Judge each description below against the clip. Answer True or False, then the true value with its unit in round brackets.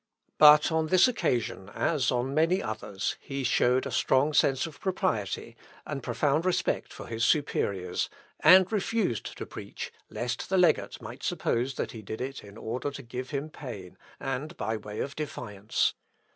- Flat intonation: False (5.2 semitones)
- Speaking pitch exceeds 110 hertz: True (135 Hz)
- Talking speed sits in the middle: True (165 wpm)